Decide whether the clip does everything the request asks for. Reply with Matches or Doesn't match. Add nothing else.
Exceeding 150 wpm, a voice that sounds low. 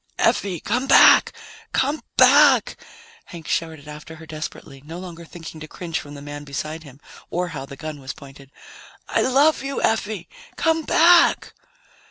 Doesn't match